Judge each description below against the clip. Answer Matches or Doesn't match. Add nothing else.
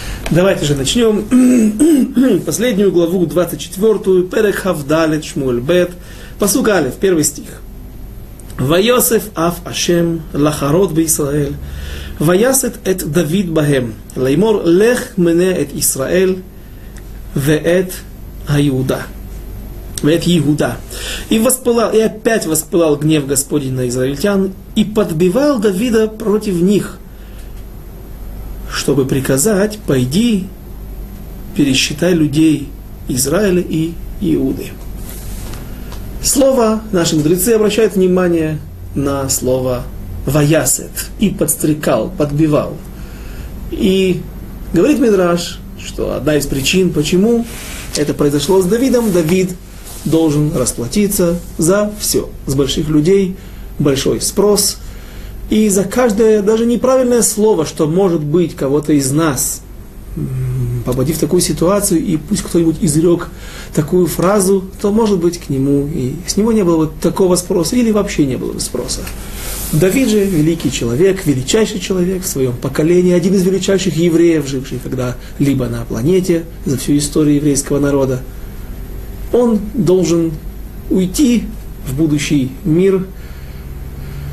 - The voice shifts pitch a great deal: Matches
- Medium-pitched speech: Matches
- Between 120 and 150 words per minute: Doesn't match